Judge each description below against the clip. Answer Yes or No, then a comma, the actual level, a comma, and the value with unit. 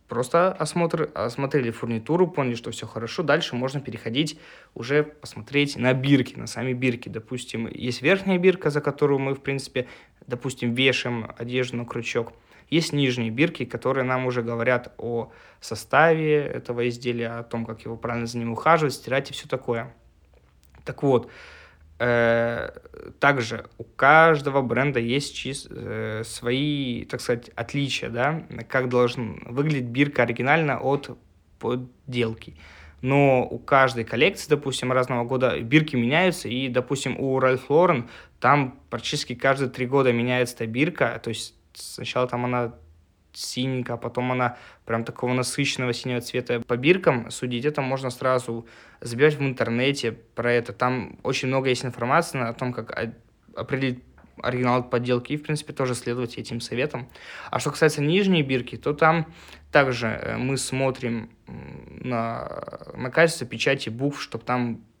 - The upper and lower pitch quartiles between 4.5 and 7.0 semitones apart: No, average, 3.0 semitones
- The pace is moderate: Yes, average, 145 wpm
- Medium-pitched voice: No, low, 125 Hz